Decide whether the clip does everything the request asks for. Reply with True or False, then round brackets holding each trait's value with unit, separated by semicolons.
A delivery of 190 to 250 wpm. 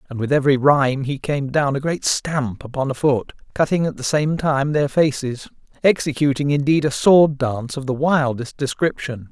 False (180 wpm)